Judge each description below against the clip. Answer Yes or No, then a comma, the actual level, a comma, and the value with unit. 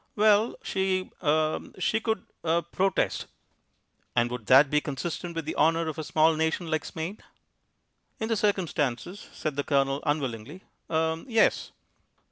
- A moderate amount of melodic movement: Yes, average, 4.1 semitones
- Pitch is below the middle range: No, medium, 160 Hz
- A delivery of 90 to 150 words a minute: Yes, average, 145 wpm